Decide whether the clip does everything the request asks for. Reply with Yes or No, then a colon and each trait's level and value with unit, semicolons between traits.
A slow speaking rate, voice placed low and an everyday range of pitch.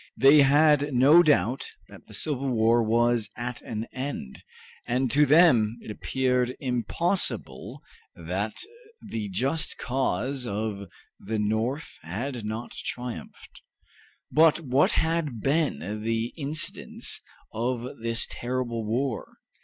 Yes: slow, 115 wpm; low, 125 Hz; average, 3.9 semitones